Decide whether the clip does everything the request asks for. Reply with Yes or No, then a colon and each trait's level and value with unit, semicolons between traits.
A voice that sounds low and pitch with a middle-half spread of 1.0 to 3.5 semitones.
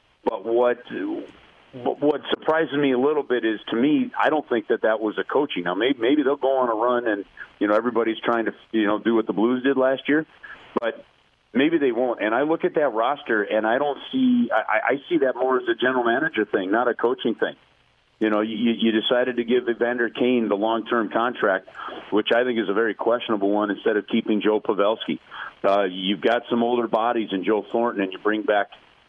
Yes: low, 120 Hz; average, 3.2 semitones